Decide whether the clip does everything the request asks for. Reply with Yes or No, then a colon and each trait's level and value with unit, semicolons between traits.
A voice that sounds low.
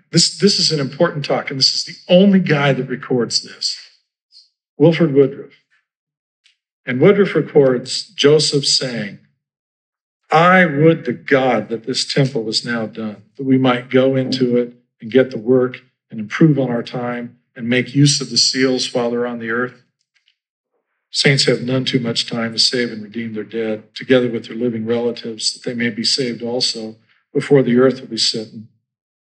Yes: low, 125 Hz